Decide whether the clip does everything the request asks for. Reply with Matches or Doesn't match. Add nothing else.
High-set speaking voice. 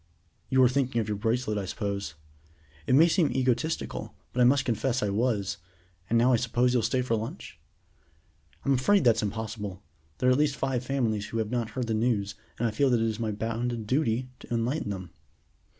Doesn't match